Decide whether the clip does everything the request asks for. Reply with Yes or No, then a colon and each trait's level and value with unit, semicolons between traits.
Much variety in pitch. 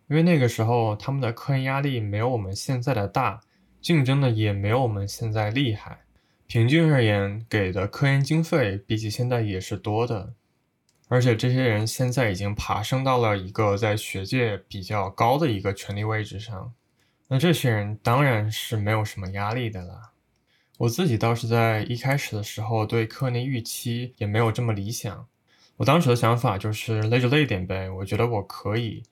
No: average, 3.2 semitones